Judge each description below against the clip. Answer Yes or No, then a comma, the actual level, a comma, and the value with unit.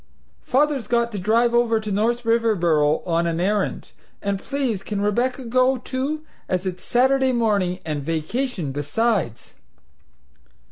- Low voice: No, high, 220 Hz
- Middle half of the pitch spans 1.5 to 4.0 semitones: No, average, 5.3 semitones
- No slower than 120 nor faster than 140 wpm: Yes, slow, 135 wpm